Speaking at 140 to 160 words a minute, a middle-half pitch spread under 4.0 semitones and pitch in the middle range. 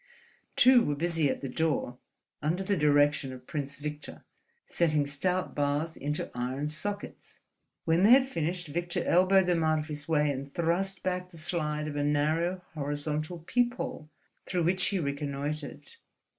Yes: average, 155 wpm; average, 3.5 semitones; medium, 155 Hz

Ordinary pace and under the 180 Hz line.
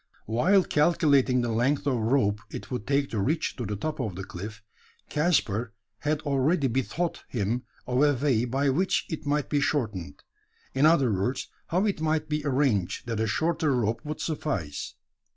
Yes: average, 175 wpm; low, 135 Hz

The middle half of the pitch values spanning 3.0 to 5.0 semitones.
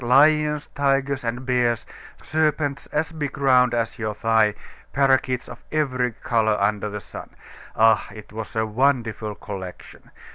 Yes: average, 4.3 semitones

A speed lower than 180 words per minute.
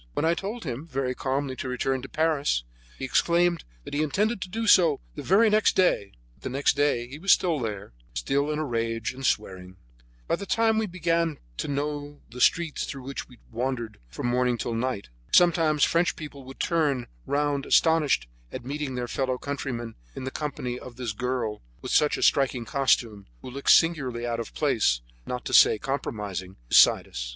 No: average, 195 wpm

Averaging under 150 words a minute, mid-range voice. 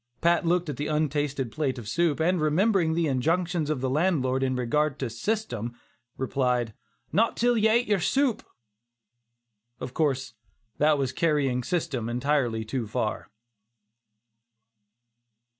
Yes: average, 140 wpm; medium, 150 Hz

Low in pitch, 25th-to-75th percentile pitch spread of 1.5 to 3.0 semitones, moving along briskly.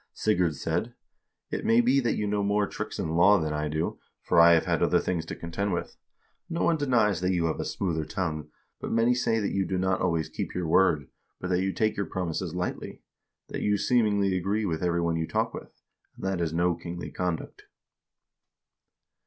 No: very low, 90 Hz; average, 3.6 semitones; fast, 210 wpm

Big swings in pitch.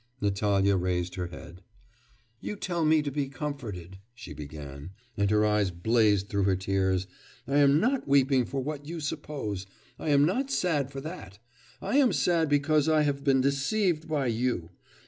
Yes: wide, 7.5 semitones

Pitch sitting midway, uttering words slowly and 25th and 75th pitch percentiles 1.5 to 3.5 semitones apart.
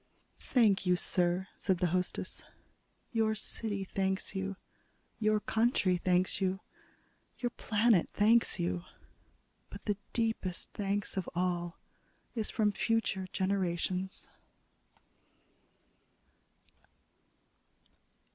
No: high, 195 Hz; slow, 90 wpm; average, 2.9 semitones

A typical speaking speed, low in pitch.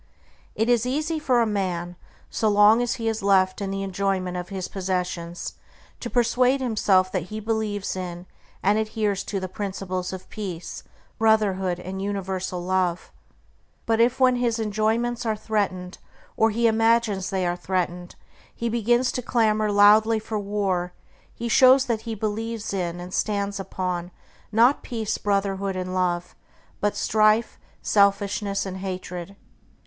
No: average, 150 wpm; high, 205 Hz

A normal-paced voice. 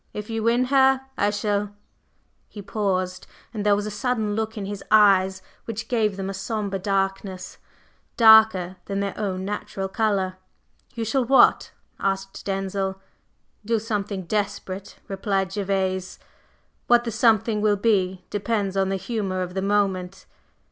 Yes: average, 150 wpm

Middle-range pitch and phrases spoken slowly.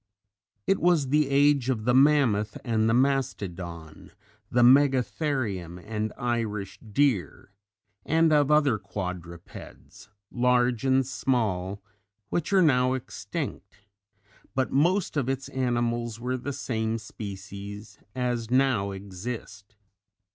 No: low, 120 Hz; slow, 110 wpm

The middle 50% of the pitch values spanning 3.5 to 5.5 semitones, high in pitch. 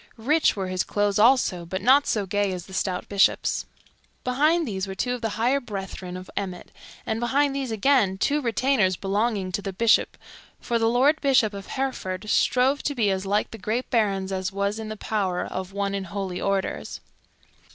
Yes: average, 4.5 semitones; high, 205 Hz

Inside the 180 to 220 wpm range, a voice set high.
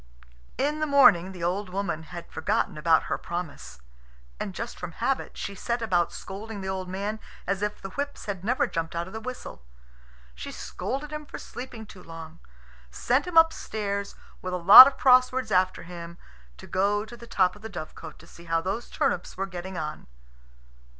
Yes: average, 190 wpm; high, 195 Hz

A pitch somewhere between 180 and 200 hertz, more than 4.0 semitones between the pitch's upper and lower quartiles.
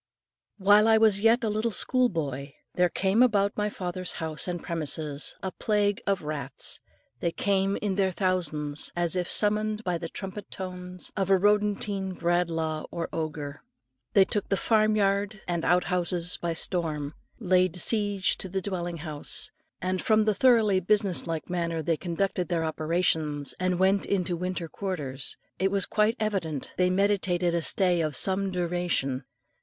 No: medium, 185 Hz; average, 3.2 semitones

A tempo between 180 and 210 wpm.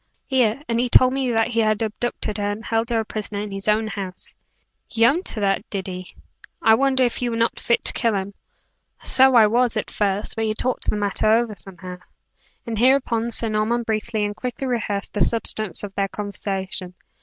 Yes: average, 200 wpm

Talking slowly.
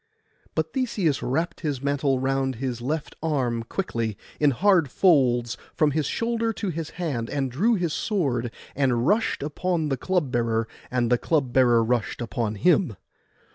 No: average, 160 wpm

